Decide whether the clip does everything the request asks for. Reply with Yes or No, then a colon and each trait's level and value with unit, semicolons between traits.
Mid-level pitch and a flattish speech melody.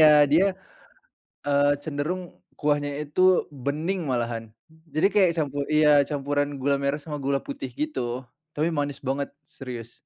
Yes: medium, 145 Hz; narrow, 1.9 semitones